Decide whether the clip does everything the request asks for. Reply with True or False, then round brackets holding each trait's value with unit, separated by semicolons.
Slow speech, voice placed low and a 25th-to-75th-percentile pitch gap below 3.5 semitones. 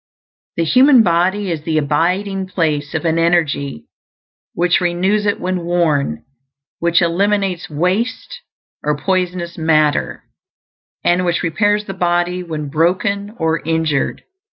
False (125 wpm; 175 Hz; 2.8 semitones)